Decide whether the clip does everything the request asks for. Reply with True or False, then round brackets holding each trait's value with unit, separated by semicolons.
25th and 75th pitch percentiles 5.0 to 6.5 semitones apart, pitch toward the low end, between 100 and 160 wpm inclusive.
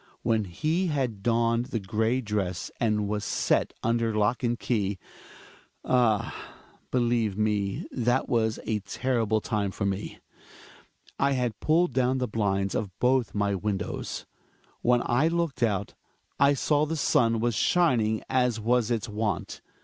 False (3.1 semitones; 115 Hz; 150 wpm)